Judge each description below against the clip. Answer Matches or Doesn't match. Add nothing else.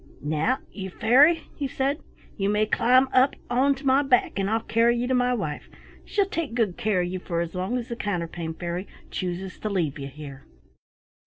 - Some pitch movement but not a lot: Doesn't match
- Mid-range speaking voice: Doesn't match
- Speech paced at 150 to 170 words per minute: Doesn't match